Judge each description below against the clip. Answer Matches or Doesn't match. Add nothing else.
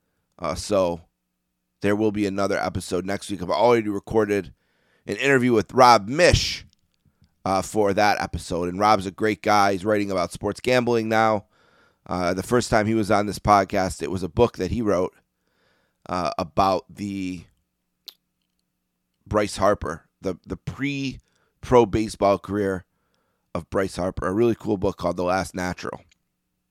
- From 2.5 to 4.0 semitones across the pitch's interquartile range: Matches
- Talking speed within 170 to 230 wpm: Doesn't match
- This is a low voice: Matches